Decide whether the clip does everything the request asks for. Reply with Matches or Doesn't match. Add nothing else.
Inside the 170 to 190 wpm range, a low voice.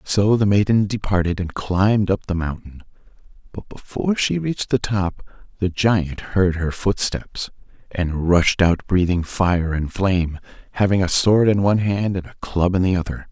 Matches